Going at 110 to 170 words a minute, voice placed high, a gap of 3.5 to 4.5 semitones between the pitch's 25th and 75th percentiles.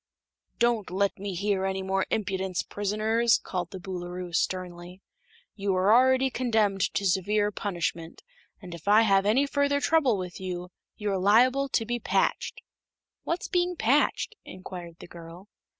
Yes: average, 150 wpm; high, 200 Hz; average, 4.0 semitones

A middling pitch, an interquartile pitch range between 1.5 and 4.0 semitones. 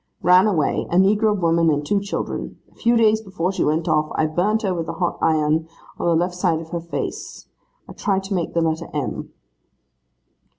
Yes: medium, 175 Hz; average, 3.4 semitones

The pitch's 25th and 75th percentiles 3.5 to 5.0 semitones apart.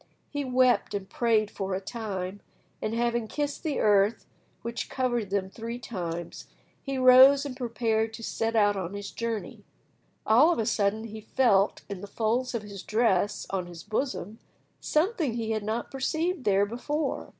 Yes: average, 3.8 semitones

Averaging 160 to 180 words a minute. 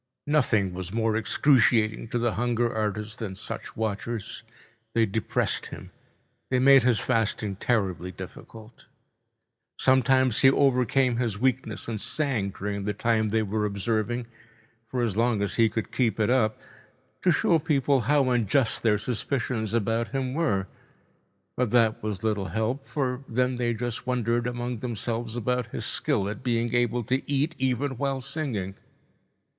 No: average, 150 wpm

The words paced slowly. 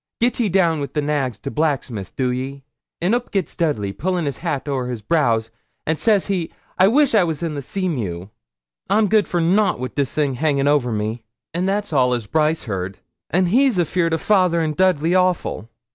No: fast, 205 wpm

